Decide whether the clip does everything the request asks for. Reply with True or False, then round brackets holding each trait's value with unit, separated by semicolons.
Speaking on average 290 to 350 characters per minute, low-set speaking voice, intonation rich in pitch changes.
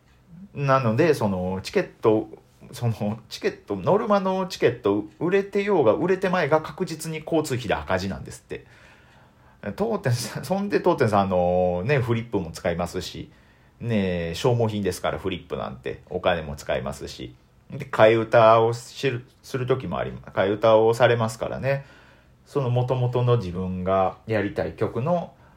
True (315 characters per minute; 115 Hz; 6.9 semitones)